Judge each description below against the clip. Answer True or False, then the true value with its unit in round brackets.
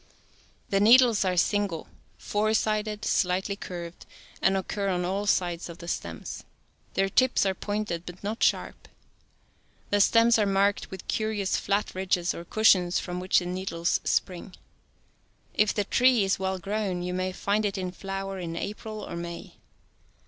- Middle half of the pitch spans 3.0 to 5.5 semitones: False (2.6 semitones)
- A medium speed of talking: True (170 wpm)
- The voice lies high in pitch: True (195 Hz)